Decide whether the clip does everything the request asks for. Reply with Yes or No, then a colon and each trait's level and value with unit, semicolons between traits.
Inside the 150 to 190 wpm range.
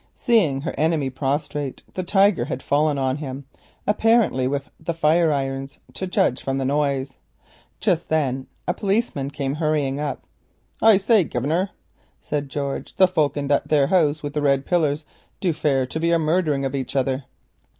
Yes: average, 165 wpm